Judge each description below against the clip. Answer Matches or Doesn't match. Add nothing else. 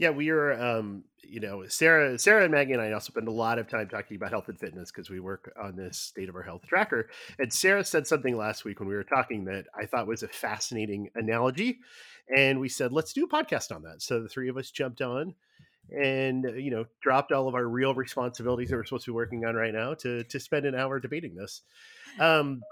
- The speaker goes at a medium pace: Doesn't match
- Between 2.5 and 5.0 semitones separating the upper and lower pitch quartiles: Matches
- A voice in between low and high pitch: Doesn't match